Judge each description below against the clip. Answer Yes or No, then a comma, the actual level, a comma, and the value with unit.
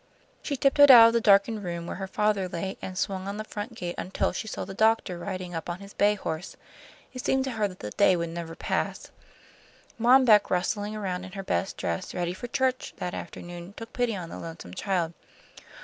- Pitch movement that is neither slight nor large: Yes, average, 3.8 semitones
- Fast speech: Yes, fast, 215 wpm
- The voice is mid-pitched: No, high, 195 Hz